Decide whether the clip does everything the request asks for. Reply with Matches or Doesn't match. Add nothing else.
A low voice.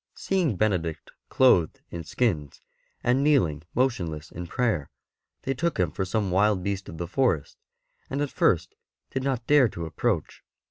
Matches